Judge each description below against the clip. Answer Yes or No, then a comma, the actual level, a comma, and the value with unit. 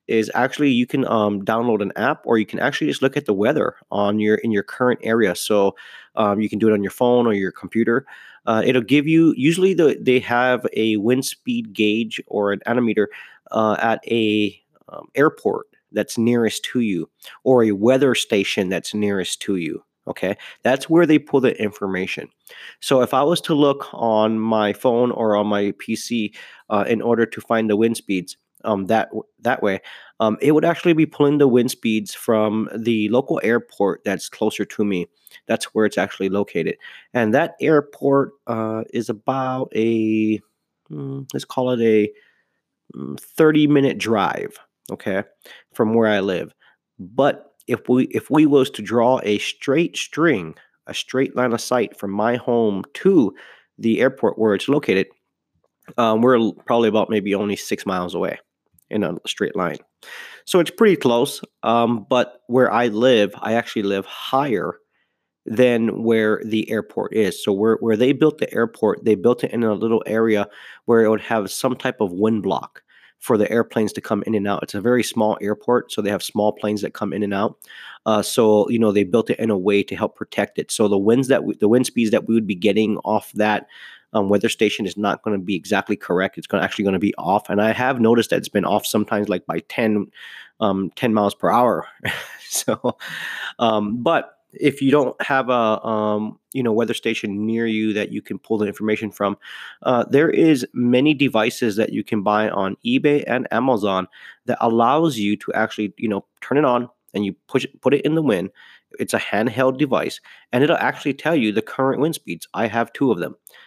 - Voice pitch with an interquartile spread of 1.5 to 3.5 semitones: Yes, average, 3.1 semitones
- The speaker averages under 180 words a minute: No, average, 200 wpm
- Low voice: Yes, low, 110 Hz